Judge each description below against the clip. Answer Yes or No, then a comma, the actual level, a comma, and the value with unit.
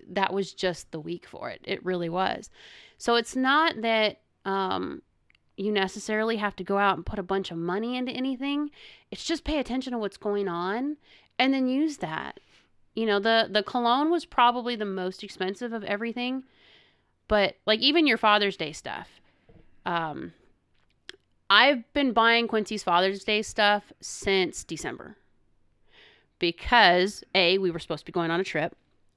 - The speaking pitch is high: Yes, high, 210 Hz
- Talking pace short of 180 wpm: Yes, average, 165 wpm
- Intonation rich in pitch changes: No, average, 4.4 semitones